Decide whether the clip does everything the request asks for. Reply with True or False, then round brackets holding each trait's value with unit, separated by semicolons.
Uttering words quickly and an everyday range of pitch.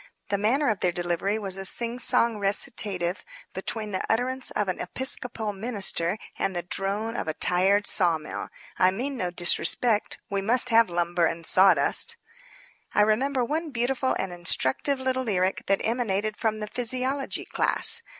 False (155 wpm; 4.7 semitones)